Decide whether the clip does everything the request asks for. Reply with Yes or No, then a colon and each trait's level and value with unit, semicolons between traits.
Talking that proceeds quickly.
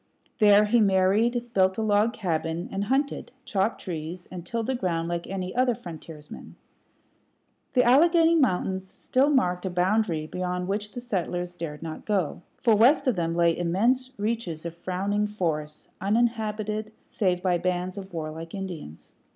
No: average, 155 wpm